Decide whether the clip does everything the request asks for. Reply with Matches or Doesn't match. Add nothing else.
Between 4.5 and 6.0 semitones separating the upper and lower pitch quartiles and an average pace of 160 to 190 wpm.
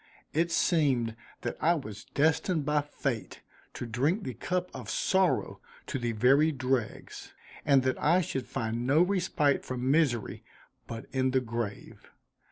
Doesn't match